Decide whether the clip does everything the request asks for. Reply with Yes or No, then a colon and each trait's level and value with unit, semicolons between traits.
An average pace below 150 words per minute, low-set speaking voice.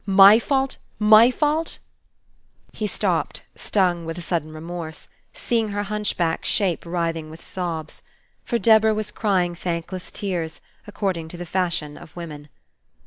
No: average, 140 wpm; medium, 180 Hz